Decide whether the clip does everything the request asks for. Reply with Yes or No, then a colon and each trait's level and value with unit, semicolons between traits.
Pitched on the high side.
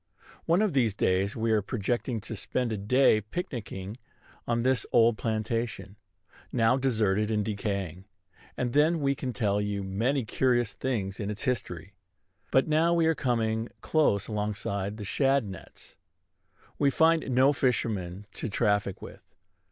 No: low, 115 Hz